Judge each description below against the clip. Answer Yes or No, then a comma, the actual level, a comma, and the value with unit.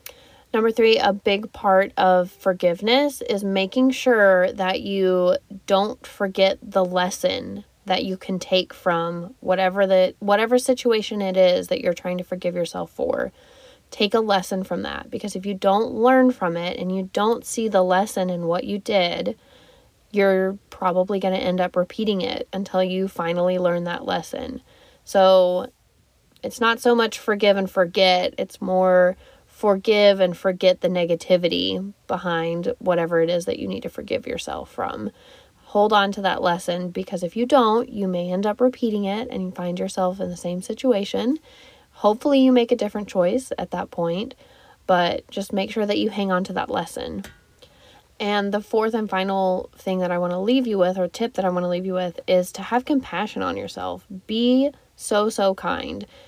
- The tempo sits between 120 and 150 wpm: No, average, 180 wpm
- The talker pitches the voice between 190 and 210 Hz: Yes, high, 195 Hz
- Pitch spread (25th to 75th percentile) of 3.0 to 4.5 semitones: Yes, average, 3.9 semitones